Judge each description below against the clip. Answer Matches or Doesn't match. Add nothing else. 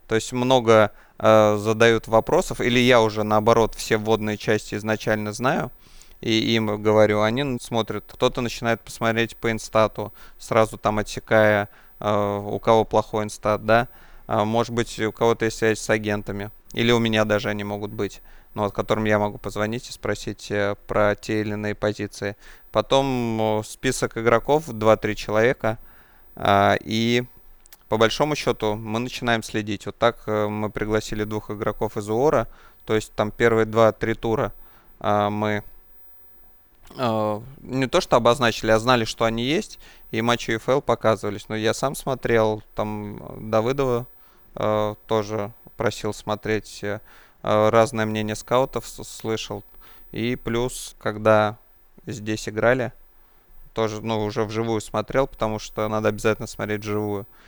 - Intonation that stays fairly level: Matches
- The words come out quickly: Doesn't match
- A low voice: Matches